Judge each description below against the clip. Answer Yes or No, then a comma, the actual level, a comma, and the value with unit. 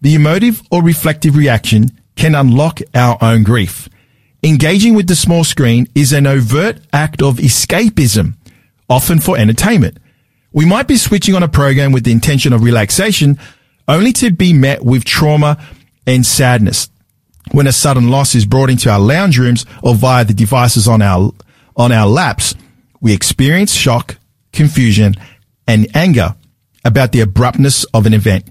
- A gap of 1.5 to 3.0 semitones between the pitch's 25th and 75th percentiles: No, average, 4.6 semitones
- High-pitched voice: No, low, 130 Hz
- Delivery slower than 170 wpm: Yes, average, 160 wpm